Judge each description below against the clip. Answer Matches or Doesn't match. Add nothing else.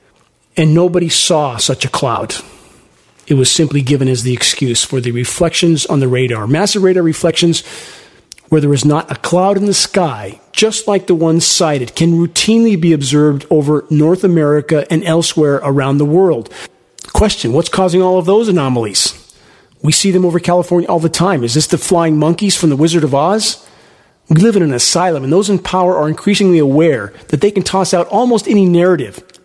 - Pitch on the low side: Doesn't match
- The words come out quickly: Doesn't match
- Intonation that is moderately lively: Matches